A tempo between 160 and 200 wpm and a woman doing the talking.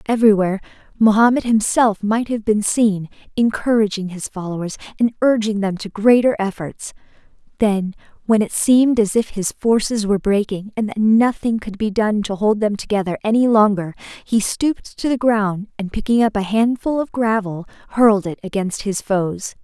Yes: average, 170 wpm; female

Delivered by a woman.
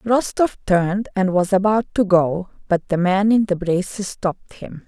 Yes: female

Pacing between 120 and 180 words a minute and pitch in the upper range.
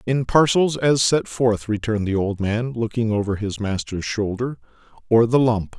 No: average, 175 wpm; low, 115 Hz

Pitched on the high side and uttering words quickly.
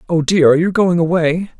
No: medium, 170 Hz; fast, 225 wpm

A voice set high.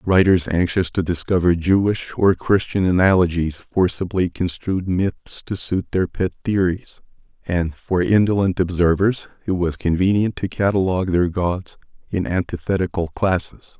No: very low, 90 Hz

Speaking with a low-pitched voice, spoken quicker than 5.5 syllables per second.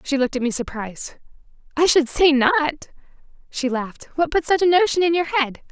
No: very high, 295 Hz; 5.7 syllables/s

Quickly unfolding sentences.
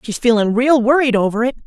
Yes: fast, 215 wpm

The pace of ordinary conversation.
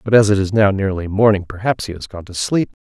No: fast, 275 wpm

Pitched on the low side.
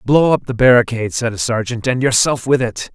Yes: low, 120 Hz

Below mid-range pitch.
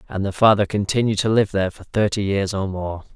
Yes: low, 100 Hz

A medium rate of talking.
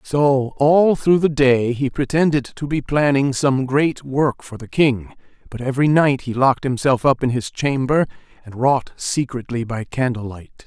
Yes: average, 180 wpm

